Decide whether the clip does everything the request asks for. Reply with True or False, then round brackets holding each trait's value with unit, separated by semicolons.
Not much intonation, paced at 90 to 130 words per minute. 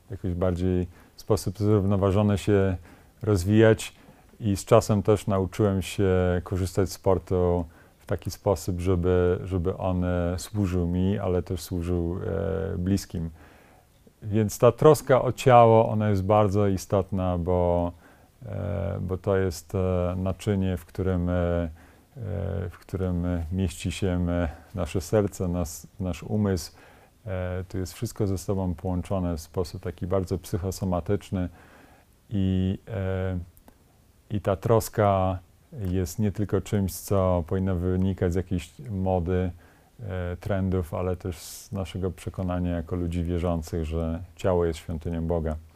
True (2.2 semitones; 125 wpm)